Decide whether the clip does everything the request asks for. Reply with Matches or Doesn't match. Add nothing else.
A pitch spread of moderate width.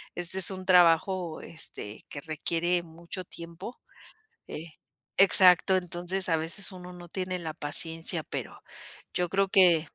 Doesn't match